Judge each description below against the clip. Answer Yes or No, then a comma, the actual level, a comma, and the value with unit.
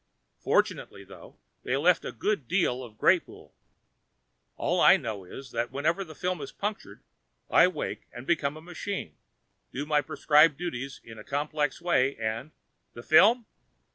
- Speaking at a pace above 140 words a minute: Yes, average, 160 wpm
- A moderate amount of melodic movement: No, wide, 6.1 semitones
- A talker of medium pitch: Yes, medium, 145 Hz